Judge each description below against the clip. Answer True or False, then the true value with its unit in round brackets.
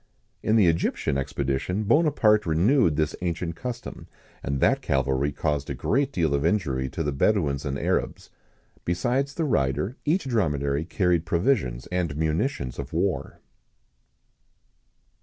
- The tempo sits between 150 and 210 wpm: False (135 wpm)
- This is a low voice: True (85 Hz)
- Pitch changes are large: True (7.3 semitones)